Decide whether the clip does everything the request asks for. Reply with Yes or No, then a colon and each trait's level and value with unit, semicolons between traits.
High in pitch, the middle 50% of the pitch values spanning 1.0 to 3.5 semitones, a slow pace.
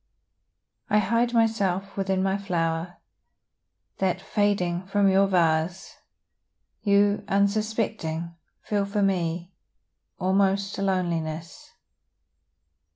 Yes: high, 195 Hz; narrow, 2.5 semitones; slow, 90 wpm